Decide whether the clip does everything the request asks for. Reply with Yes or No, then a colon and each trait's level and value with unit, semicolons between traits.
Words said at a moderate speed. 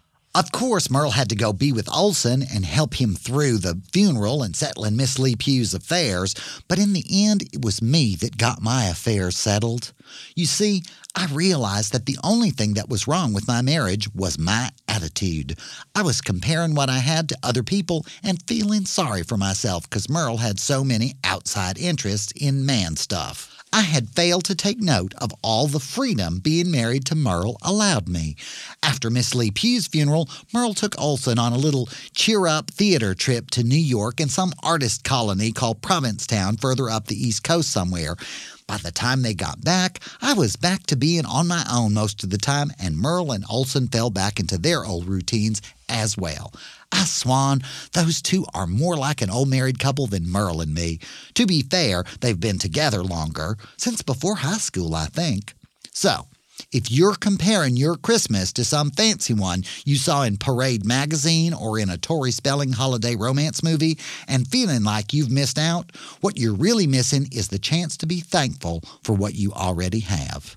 Yes: average, 190 wpm